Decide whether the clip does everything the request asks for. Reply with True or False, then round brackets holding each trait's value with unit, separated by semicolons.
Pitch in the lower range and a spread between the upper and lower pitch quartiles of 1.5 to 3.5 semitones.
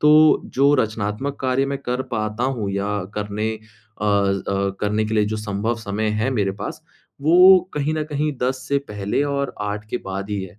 False (110 Hz; 4.6 semitones)